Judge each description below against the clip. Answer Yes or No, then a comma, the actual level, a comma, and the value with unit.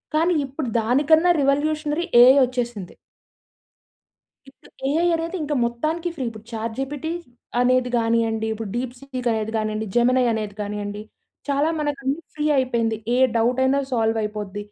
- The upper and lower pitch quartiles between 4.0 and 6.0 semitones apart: Yes, average, 4.5 semitones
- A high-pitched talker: Yes, very high, 250 Hz